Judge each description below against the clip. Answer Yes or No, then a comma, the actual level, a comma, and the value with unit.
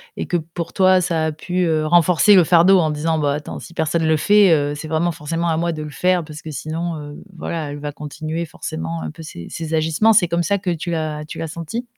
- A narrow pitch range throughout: Yes, narrow, 2.2 semitones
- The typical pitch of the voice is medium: Yes, medium, 160 Hz